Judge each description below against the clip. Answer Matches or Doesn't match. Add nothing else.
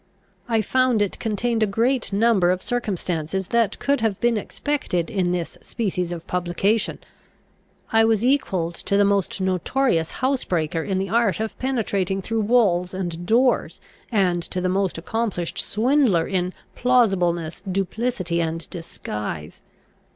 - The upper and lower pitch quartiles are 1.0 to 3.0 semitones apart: Doesn't match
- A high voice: Matches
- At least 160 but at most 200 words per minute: Doesn't match